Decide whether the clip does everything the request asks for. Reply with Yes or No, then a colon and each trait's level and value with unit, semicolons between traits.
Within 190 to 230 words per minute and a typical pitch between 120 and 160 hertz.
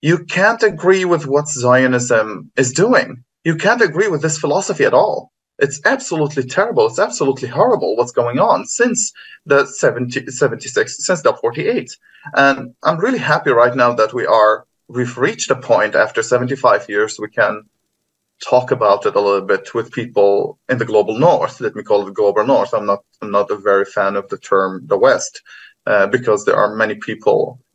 Yes: average, 195 wpm; low, 135 Hz